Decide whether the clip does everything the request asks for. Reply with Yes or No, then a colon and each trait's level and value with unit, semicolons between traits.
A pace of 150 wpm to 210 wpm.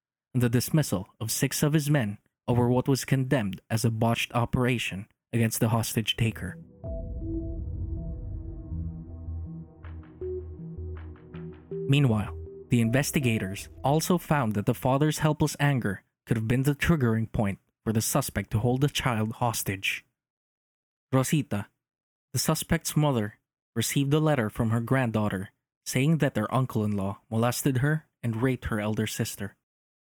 No: slow, 135 wpm